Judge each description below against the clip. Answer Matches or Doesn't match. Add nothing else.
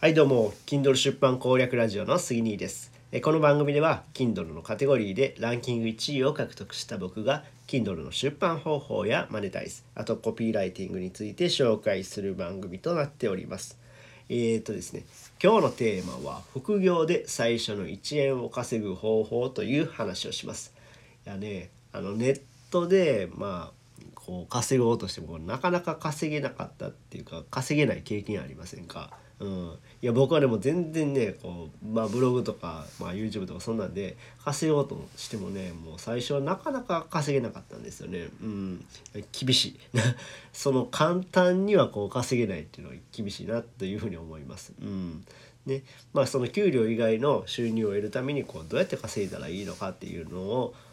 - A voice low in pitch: Matches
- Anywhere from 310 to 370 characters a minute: Doesn't match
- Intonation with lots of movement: Doesn't match